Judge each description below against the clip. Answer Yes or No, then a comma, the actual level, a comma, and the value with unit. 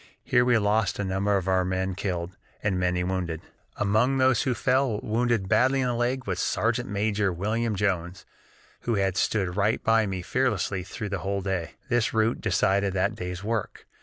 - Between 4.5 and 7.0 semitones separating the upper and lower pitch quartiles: No, average, 3.8 semitones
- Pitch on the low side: Yes, low, 100 Hz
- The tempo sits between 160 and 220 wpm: Yes, average, 185 wpm